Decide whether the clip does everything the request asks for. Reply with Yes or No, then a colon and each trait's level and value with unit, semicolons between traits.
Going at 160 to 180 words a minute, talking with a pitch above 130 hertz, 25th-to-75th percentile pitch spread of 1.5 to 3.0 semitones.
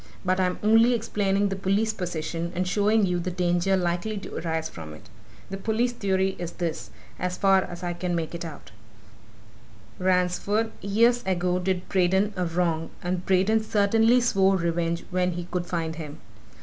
Yes: average, 170 wpm; medium, 185 Hz; narrow, 2.5 semitones